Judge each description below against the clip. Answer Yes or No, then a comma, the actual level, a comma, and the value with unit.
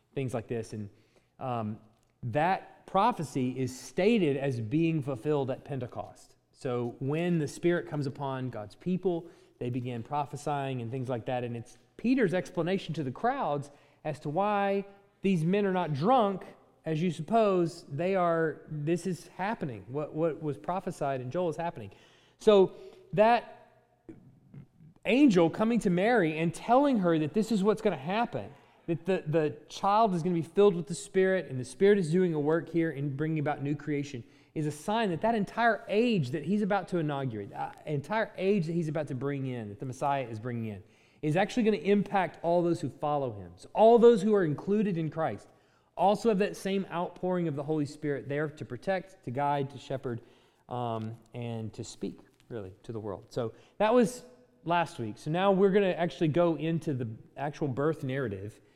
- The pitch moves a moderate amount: No, wide, 6.0 semitones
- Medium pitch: Yes, medium, 160 Hz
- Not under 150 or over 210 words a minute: Yes, average, 190 wpm